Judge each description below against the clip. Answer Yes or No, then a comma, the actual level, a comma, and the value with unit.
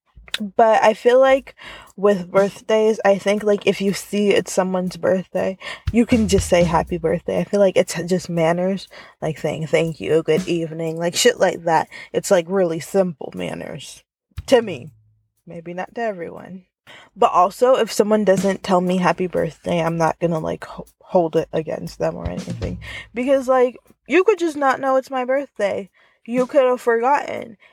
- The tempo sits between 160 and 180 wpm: Yes, average, 175 wpm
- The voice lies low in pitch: No, high, 190 Hz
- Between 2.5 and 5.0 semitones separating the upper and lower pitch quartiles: No, wide, 5.4 semitones